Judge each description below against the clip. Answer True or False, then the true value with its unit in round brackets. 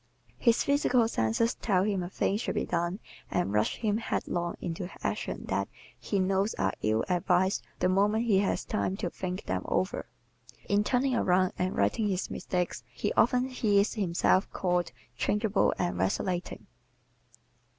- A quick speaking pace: False (155 wpm)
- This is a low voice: False (190 Hz)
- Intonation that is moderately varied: True (3.1 semitones)